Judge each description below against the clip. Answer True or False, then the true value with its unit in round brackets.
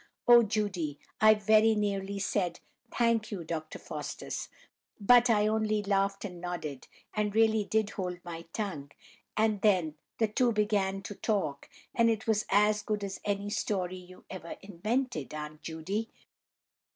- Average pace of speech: True (150 wpm)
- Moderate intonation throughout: True (3.2 semitones)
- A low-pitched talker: False (205 Hz)